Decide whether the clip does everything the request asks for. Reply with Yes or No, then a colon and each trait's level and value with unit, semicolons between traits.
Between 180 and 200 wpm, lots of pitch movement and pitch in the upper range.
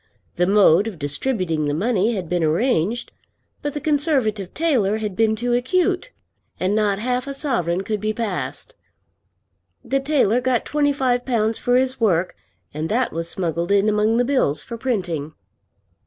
No: average, 165 wpm; wide, 5.8 semitones; high, 220 Hz